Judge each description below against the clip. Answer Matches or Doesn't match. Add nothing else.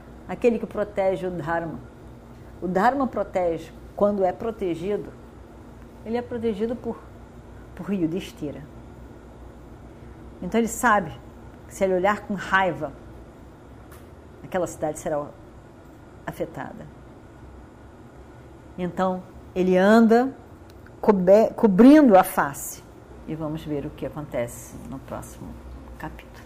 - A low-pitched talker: Doesn't match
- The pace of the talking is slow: Matches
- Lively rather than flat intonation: Matches